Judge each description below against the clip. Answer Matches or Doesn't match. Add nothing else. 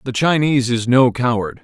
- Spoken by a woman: Doesn't match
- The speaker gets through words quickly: Doesn't match